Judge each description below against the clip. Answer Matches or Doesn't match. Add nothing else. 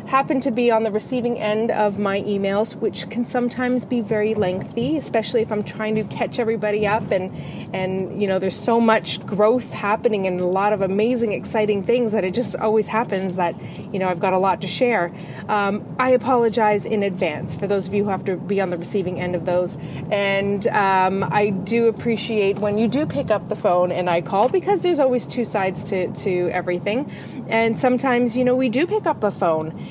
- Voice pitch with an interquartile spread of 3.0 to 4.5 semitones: Matches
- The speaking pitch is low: Doesn't match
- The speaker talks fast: Matches